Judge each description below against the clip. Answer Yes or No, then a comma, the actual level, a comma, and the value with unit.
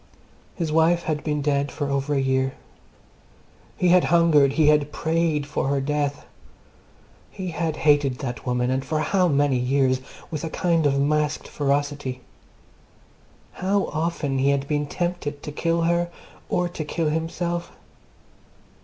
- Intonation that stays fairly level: No, average, 3.1 semitones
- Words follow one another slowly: No, average, 150 wpm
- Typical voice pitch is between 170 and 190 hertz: No, medium, 150 Hz